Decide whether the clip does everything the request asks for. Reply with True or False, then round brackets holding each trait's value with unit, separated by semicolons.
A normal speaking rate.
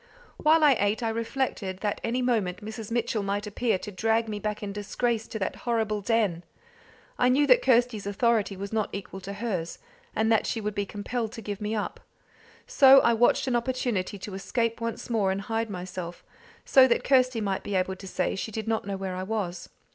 False (210 wpm)